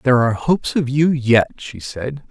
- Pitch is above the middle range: No, low, 130 Hz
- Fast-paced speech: Yes, fast, 210 wpm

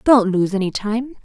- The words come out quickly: No, average, 195 wpm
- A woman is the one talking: Yes, female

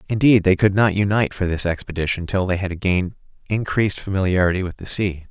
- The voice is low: Yes, very low, 95 Hz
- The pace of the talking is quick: No, average, 190 wpm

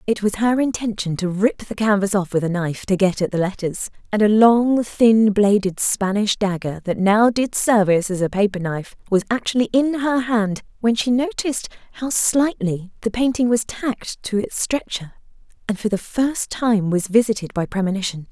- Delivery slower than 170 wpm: No, average, 190 wpm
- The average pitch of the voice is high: Yes, high, 210 Hz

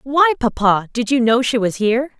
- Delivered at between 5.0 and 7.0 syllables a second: Yes, 5.1 syllables/s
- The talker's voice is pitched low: No, high, 240 Hz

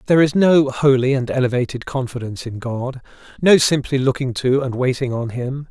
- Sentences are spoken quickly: No, average, 180 wpm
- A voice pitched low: Yes, low, 130 Hz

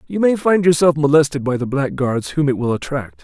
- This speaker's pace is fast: Yes, fast, 220 wpm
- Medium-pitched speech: Yes, medium, 145 Hz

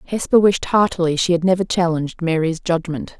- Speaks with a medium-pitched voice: Yes, medium, 175 Hz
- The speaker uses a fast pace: No, average, 170 wpm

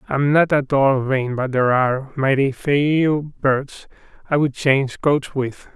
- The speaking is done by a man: Yes, male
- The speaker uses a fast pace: No, average, 165 wpm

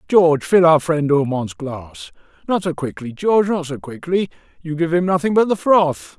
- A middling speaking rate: Yes, average, 195 wpm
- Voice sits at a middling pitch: Yes, medium, 155 Hz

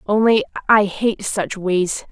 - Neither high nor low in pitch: No, high, 205 Hz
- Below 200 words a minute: Yes, average, 140 wpm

